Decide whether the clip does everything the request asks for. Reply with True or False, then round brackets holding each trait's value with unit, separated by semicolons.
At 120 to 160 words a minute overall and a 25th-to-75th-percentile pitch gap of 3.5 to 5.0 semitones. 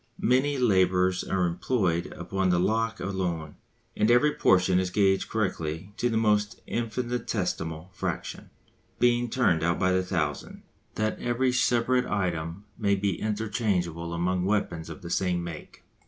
True (140 wpm; 4.4 semitones)